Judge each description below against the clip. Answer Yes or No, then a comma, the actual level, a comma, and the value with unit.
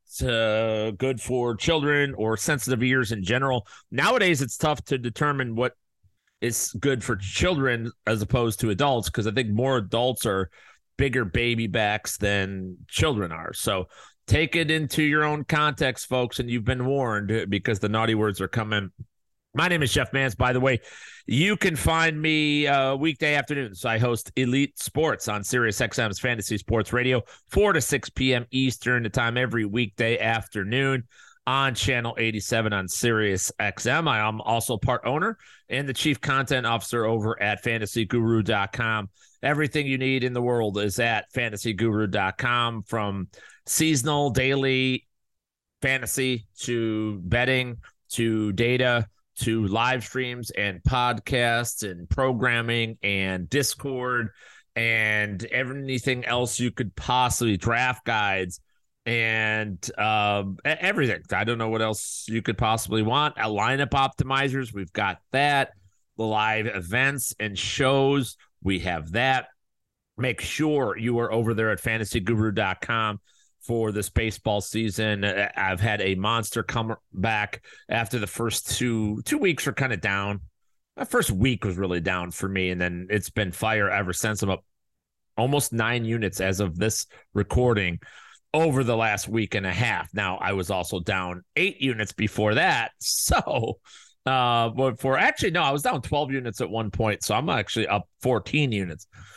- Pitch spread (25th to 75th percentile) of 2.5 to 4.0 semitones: Yes, average, 3.6 semitones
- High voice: No, low, 115 Hz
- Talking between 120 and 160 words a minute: Yes, average, 155 wpm